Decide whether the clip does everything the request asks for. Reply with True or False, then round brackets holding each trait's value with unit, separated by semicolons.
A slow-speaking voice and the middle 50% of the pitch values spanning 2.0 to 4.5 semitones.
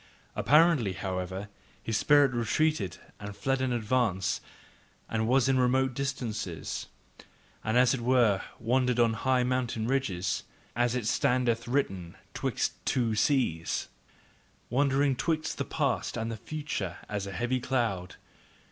True (130 wpm; 4.0 semitones)